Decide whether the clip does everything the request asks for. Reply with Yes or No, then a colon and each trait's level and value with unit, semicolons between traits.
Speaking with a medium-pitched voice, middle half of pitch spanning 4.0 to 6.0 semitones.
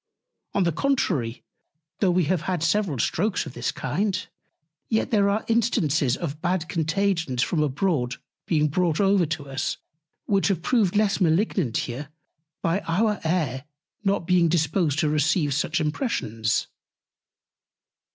Yes: medium, 170 Hz; average, 4.8 semitones